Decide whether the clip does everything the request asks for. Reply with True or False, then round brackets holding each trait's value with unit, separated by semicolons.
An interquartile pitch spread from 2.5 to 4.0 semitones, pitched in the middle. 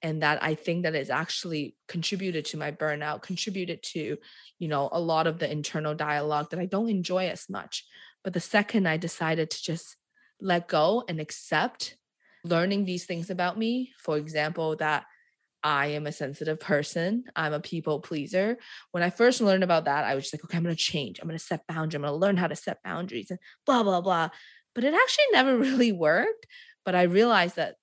True (3.7 semitones; 170 Hz)